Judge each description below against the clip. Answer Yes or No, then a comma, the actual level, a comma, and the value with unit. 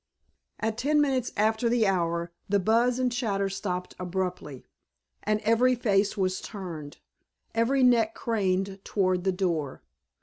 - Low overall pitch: No, high, 200 Hz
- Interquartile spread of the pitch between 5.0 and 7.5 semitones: No, average, 4.0 semitones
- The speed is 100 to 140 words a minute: Yes, slow, 135 wpm